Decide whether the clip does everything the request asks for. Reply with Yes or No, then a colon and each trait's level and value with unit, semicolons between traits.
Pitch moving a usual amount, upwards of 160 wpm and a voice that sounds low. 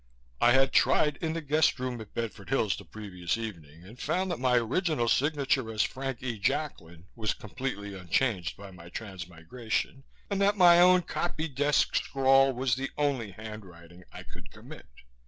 No: wide, 5.8 semitones; average, 170 wpm; low, 120 Hz